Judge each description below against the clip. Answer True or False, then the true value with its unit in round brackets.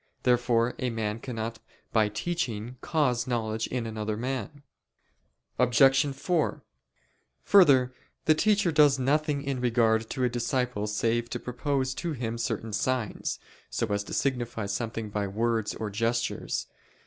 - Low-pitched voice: True (120 Hz)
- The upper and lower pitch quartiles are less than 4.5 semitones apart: True (3.2 semitones)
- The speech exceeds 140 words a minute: False (135 wpm)